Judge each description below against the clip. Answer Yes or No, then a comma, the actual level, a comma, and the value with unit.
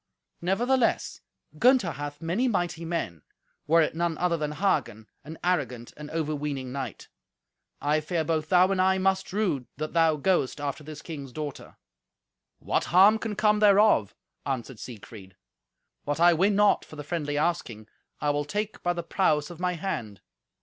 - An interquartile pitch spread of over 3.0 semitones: Yes, average, 4.3 semitones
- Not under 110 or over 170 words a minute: Yes, average, 165 wpm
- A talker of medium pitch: Yes, medium, 160 Hz